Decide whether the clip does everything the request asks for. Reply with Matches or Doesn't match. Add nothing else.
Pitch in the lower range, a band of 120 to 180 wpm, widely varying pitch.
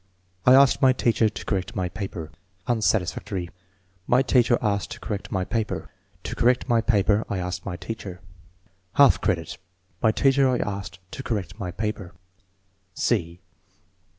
Doesn't match